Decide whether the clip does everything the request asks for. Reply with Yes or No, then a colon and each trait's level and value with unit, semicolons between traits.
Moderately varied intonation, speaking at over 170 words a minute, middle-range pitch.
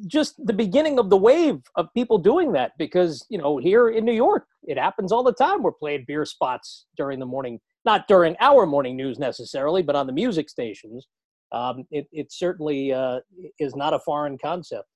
No: wide, 8.8 semitones; average, 200 wpm; medium, 165 Hz